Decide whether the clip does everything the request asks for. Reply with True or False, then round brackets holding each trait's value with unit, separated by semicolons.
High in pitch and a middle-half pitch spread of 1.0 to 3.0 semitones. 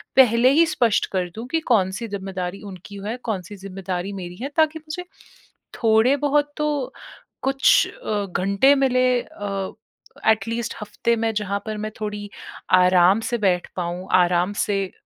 False (210 Hz; 4.6 semitones)